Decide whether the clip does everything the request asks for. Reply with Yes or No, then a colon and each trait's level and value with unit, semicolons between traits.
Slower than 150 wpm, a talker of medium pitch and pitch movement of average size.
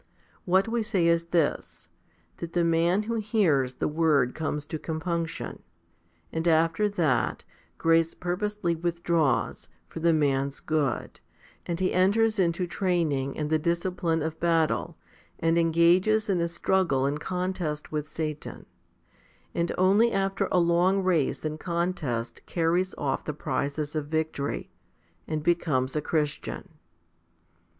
Yes: slow, 135 wpm; medium, 165 Hz; average, 3.0 semitones